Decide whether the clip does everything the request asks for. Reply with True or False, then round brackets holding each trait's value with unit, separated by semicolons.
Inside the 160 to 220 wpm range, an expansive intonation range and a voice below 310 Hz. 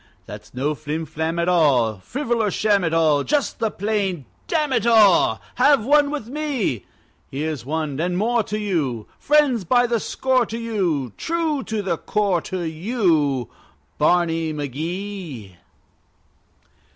False (145 wpm; 7.2 semitones; 185 Hz)